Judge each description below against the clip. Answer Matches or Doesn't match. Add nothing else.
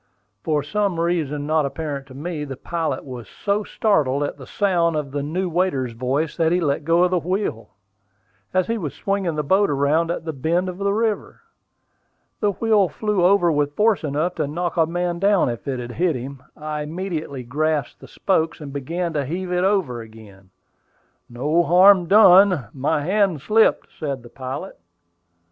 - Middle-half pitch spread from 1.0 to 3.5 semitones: Doesn't match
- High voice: Doesn't match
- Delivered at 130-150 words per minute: Doesn't match